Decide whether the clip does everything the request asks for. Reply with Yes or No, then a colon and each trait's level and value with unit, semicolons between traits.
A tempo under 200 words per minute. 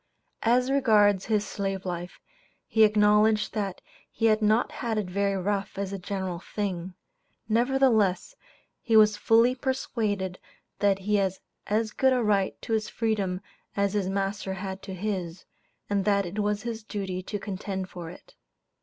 Yes: average, 160 wpm